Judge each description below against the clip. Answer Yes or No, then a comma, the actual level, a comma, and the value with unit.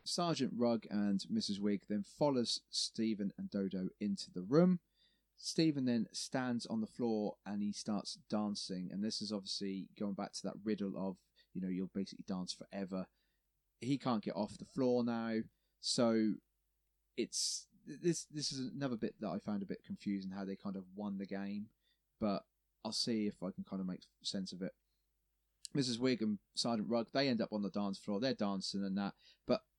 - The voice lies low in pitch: Yes, low, 105 Hz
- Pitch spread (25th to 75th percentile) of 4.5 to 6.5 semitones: Yes, average, 4.8 semitones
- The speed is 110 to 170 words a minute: No, average, 190 wpm